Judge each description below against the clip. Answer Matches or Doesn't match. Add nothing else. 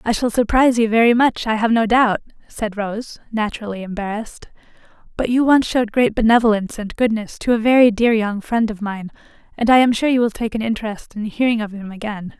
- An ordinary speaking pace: Doesn't match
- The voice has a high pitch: Matches